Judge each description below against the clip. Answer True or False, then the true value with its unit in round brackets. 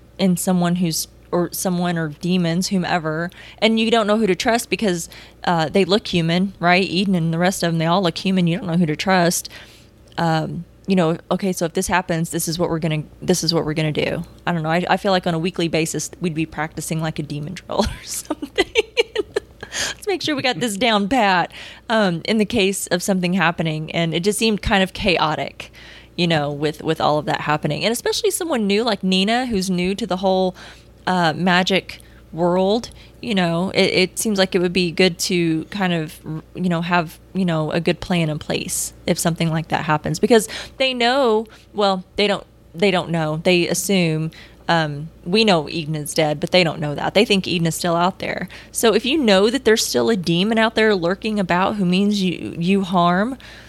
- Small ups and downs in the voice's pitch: False (3.4 semitones)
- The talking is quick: True (220 wpm)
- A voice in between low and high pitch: True (180 Hz)